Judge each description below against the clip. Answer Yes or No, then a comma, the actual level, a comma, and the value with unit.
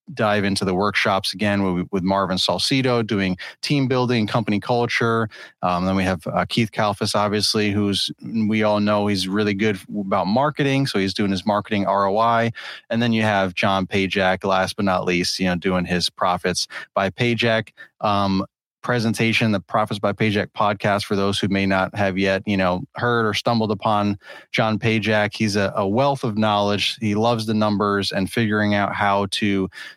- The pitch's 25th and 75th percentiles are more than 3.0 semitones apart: No, narrow, 2.4 semitones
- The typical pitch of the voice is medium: No, low, 105 Hz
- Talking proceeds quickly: No, average, 180 wpm